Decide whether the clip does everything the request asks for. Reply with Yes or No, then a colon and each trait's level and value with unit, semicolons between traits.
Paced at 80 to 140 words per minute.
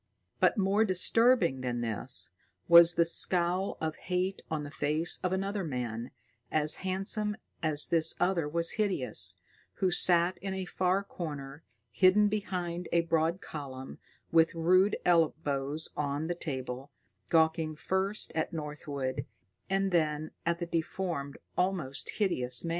Yes: slow, 135 wpm